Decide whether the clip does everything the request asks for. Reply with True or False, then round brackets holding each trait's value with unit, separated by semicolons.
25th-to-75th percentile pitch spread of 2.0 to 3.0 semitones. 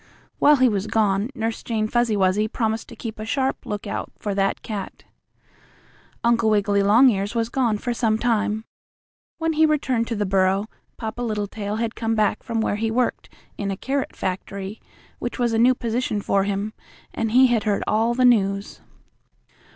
True (2.7 semitones)